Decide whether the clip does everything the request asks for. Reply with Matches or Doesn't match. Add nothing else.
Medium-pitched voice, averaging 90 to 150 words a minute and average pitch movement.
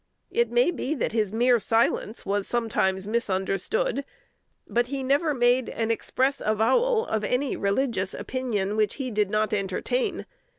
Doesn't match